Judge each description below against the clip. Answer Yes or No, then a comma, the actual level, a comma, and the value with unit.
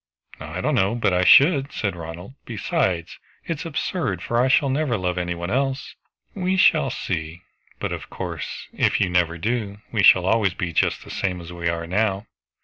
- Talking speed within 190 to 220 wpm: Yes, average, 195 wpm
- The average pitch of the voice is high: No, very low, 95 Hz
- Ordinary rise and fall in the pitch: No, wide, 6.6 semitones